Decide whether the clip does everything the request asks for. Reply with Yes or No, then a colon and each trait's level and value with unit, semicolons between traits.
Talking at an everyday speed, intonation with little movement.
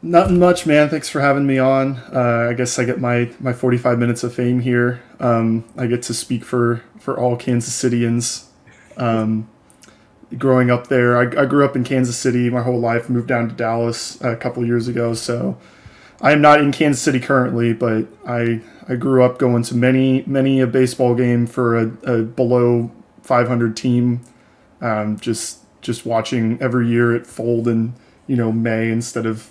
Yes: average, 190 wpm; narrow, 1.5 semitones